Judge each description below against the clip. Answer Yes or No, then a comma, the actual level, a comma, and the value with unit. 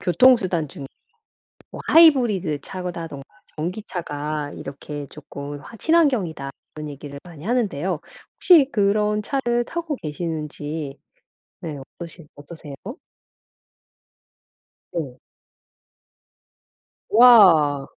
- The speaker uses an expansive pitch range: Yes, wide, 6.4 semitones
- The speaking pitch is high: No, medium, 165 Hz